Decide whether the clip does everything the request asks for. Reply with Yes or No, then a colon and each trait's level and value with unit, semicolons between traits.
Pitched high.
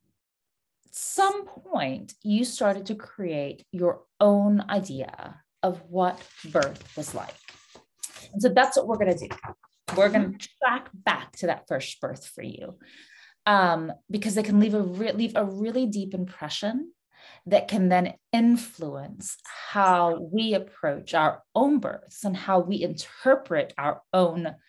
Yes: high, 205 Hz